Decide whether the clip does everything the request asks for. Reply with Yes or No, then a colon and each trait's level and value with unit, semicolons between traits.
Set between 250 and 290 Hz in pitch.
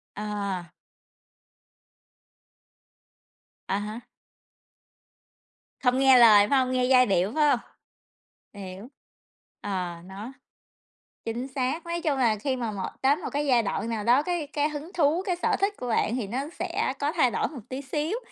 Yes: very high, 255 Hz